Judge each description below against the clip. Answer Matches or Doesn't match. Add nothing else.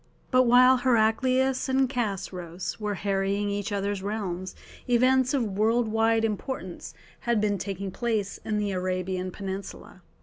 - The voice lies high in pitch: Matches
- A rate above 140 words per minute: Doesn't match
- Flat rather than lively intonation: Doesn't match